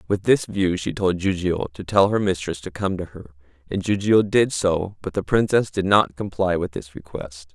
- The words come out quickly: Yes, fast, 215 wpm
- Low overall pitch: Yes, very low, 90 Hz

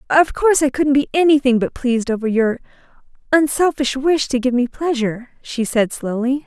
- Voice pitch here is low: No, very high, 265 Hz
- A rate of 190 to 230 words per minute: No, average, 175 wpm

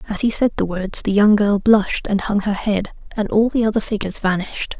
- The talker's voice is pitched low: No, high, 205 Hz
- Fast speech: Yes, fast, 240 wpm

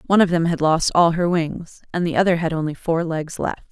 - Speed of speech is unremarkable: No, fast, 260 wpm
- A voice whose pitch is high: No, medium, 165 Hz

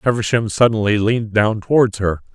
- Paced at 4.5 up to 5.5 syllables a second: Yes, 5.4 syllables/s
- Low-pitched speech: Yes, low, 110 Hz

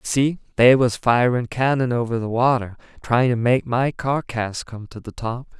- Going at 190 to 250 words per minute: Yes, average, 195 wpm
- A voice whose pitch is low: Yes, low, 120 Hz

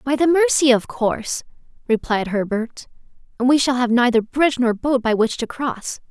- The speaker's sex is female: Yes, female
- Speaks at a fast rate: No, average, 185 wpm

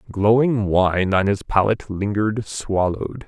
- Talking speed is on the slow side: Yes, slow, 130 wpm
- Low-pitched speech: Yes, low, 105 Hz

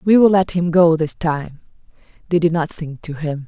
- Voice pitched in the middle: Yes, medium, 165 Hz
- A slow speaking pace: No, fast, 205 wpm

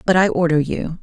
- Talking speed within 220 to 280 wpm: Yes, fast, 235 wpm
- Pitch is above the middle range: No, medium, 165 Hz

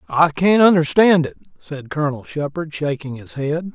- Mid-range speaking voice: Yes, medium, 150 Hz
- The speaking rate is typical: Yes, average, 160 wpm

